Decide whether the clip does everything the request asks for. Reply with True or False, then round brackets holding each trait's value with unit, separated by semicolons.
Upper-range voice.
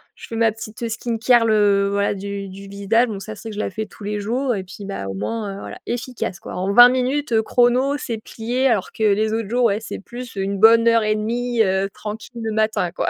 True (220 Hz)